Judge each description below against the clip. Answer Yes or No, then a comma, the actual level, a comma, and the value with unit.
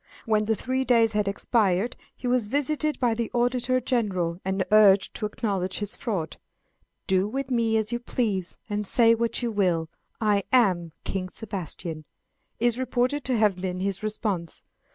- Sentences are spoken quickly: No, average, 165 wpm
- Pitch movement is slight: No, average, 4.0 semitones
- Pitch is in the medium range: No, high, 215 Hz